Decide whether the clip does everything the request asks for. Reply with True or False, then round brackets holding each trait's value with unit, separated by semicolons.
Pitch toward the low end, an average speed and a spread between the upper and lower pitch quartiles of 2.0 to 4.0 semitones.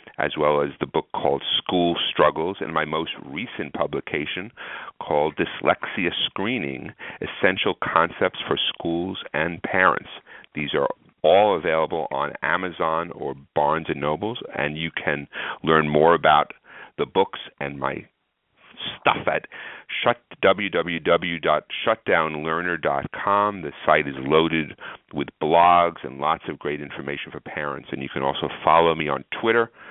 False (80 Hz; 130 wpm; 2.7 semitones)